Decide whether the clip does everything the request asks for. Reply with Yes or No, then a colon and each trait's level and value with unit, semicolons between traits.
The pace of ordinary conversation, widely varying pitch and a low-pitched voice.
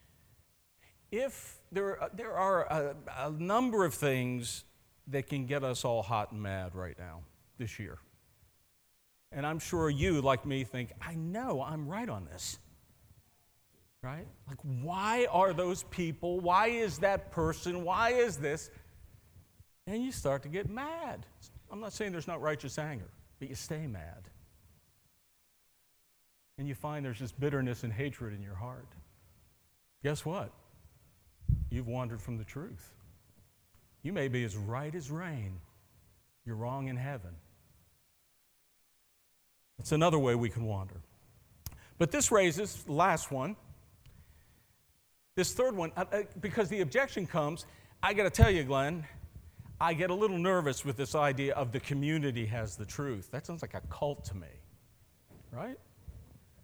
Yes: average, 150 wpm; wide, 8.2 semitones; low, 130 Hz